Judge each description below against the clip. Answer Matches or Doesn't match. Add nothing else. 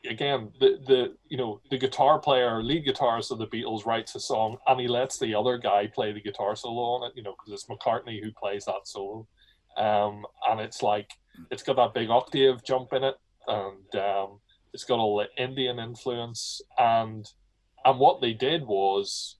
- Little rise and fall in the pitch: Doesn't match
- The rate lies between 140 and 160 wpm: Doesn't match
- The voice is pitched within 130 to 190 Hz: Doesn't match